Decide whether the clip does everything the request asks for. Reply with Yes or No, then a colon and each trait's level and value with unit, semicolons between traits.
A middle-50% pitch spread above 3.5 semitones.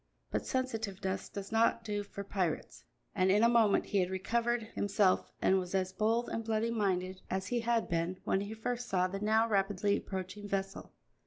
No: average, 3.0 semitones